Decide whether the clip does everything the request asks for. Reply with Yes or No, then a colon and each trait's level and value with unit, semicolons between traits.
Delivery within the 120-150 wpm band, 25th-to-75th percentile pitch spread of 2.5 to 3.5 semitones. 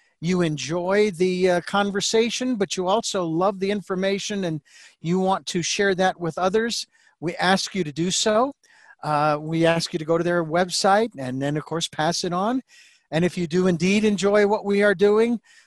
No: average, 190 wpm; average, 3.2 semitones